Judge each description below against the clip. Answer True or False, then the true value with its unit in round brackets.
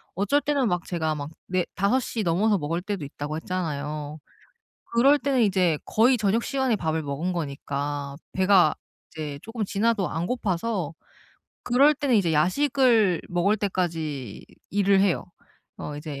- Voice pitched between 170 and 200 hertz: True (185 Hz)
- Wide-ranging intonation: True (6.2 semitones)